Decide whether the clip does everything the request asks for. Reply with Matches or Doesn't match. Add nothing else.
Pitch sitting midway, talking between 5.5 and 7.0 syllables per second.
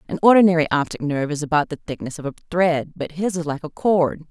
Matches